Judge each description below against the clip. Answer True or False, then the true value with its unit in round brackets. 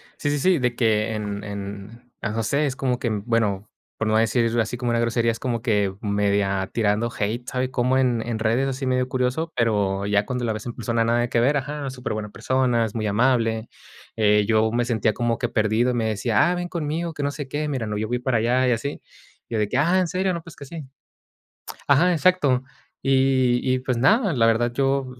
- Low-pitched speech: True (120 Hz)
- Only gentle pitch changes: False (3.3 semitones)